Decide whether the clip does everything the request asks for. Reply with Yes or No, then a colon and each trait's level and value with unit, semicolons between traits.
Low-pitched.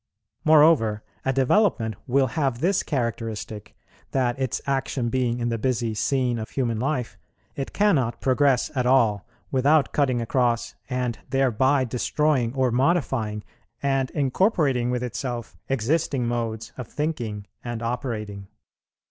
Yes: low, 125 Hz